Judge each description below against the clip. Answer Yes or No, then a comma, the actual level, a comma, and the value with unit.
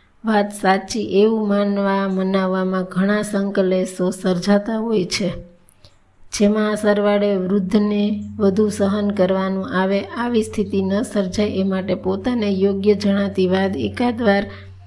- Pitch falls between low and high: No, high, 200 Hz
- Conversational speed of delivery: Yes, average, 115 wpm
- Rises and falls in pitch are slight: Yes, narrow, 1.8 semitones